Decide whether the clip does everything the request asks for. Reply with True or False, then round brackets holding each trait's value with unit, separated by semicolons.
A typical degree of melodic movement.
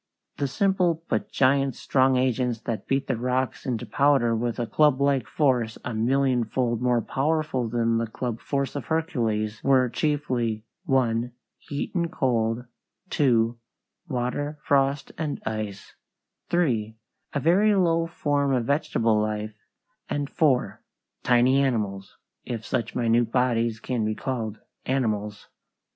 True (3.7 semitones)